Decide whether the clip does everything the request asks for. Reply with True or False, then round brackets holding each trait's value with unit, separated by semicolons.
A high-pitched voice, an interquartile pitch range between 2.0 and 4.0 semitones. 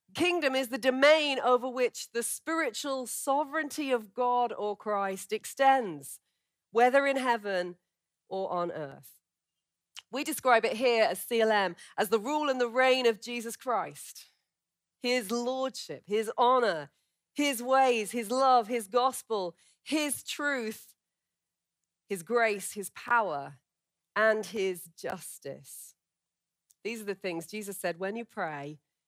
False (235 Hz; 4.7 semitones)